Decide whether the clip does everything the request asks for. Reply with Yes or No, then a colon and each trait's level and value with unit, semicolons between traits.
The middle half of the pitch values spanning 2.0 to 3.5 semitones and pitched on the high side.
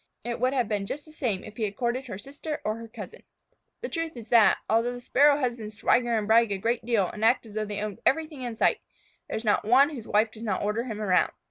Yes: average, 3.0 semitones; high, 230 Hz